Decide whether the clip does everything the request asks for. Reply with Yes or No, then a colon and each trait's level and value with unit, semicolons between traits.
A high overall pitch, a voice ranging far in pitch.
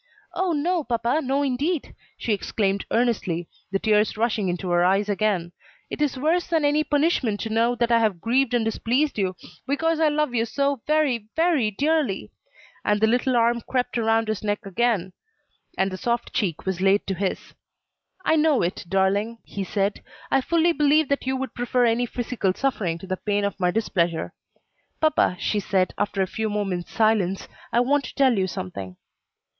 Yes: high, 225 Hz; wide, 5.8 semitones